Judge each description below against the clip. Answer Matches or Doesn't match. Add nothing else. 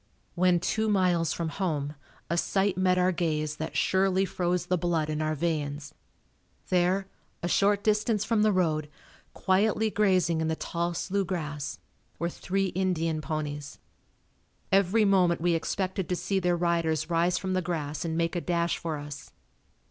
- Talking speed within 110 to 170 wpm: Matches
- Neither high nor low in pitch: Matches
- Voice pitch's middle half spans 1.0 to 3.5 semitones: Matches